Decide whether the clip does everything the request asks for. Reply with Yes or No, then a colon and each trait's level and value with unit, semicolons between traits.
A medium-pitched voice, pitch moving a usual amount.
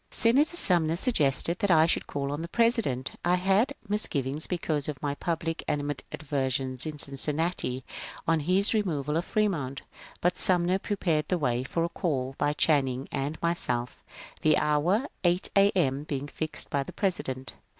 Yes: medium, 155 Hz; average, 4.6 semitones